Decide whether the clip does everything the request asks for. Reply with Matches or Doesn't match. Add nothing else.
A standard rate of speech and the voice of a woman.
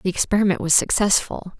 Matches